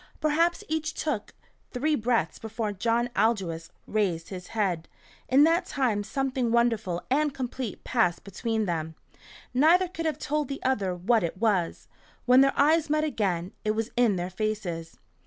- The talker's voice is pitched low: No, high, 230 Hz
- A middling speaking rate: Yes, average, 155 wpm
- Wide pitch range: Yes, wide, 6.5 semitones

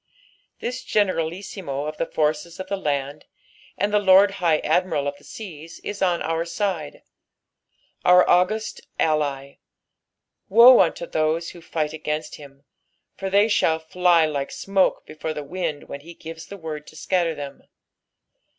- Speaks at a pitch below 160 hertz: No, medium, 165 Hz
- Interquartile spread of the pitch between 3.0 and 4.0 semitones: Yes, average, 3.7 semitones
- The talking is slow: No, average, 155 wpm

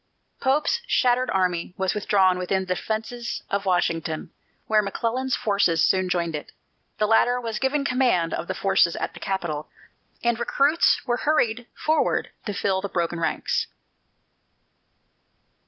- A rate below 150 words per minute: Yes, average, 140 wpm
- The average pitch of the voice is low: No, high, 200 Hz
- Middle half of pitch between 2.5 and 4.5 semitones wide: No, average, 5.2 semitones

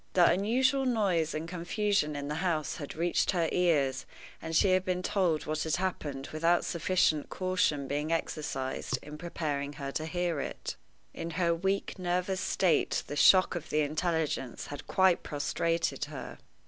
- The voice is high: No, medium, 165 Hz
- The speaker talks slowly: No, average, 160 wpm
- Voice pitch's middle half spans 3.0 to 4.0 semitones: Yes, average, 3.5 semitones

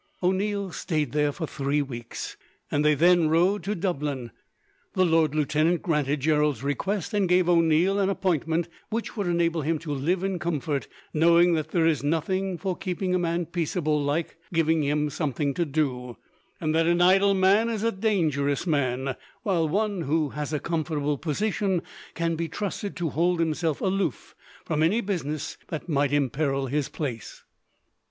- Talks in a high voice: No, medium, 165 Hz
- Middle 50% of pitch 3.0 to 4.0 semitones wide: Yes, average, 3.6 semitones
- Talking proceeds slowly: No, average, 165 wpm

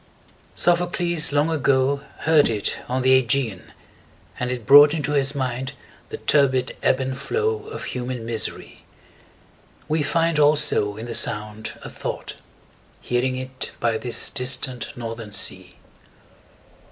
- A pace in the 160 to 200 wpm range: No, average, 140 wpm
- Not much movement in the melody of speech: No, average, 3.6 semitones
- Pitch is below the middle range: Yes, low, 130 Hz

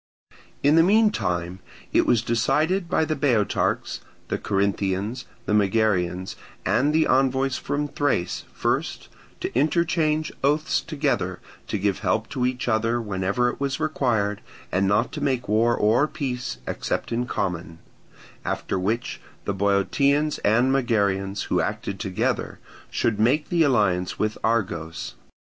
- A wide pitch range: Yes, wide, 6.0 semitones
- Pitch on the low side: Yes, low, 115 Hz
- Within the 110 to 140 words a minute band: Yes, slow, 135 wpm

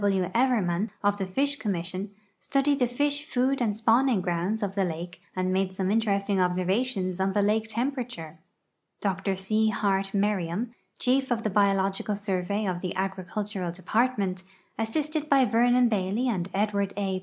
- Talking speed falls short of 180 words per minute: Yes, average, 160 wpm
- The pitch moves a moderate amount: Yes, average, 4.0 semitones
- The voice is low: No, high, 205 Hz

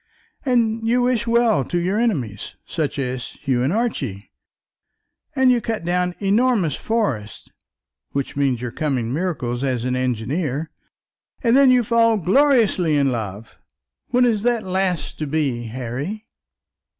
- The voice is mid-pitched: Yes, medium, 175 Hz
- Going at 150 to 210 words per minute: No, average, 140 wpm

